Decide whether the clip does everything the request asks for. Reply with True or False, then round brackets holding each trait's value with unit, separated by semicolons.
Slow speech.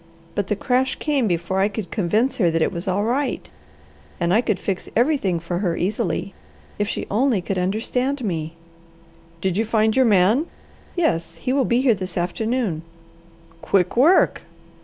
False (170 wpm)